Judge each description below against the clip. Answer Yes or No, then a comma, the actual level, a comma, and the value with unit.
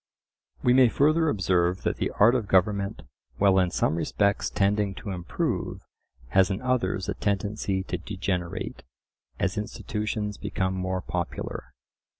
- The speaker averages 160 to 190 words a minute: No, average, 140 wpm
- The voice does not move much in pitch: Yes, narrow, 2.2 semitones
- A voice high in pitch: No, low, 100 Hz